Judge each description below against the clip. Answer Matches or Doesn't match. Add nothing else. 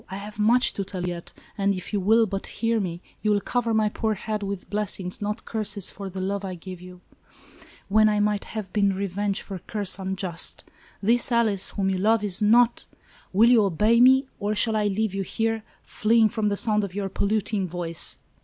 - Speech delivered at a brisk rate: Matches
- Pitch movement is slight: Matches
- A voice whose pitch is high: Matches